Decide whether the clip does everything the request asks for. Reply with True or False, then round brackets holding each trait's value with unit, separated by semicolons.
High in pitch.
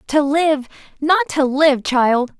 True (275 Hz)